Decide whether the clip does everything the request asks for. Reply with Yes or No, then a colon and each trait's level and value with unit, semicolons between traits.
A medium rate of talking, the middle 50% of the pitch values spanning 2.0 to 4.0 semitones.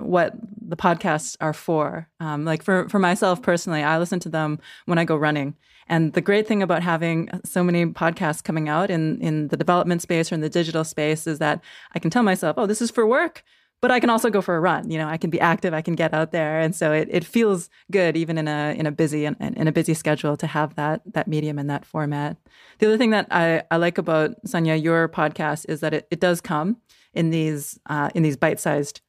No: fast, 245 wpm; average, 2.9 semitones